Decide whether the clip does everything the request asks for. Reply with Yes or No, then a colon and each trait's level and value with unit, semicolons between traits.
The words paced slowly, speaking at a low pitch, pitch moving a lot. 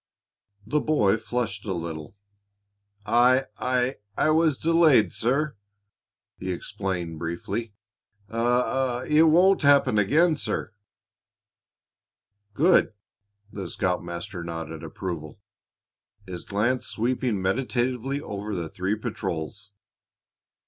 Yes: slow, 95 wpm; low, 110 Hz; wide, 5.8 semitones